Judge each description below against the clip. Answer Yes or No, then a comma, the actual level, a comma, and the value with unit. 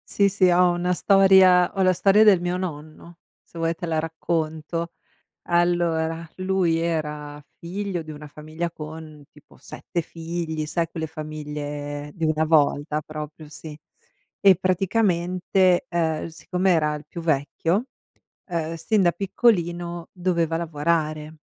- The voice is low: No, medium, 165 Hz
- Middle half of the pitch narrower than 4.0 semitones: Yes, narrow, 2.6 semitones